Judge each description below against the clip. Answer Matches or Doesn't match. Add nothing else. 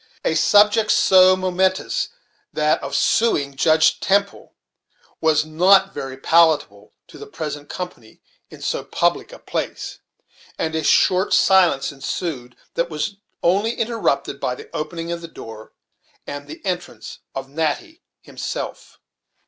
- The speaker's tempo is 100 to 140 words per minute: Matches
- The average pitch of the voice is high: Doesn't match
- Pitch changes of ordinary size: Matches